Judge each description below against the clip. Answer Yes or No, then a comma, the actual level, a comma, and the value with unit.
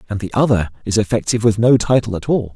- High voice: No, low, 110 Hz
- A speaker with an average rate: No, fast, 235 wpm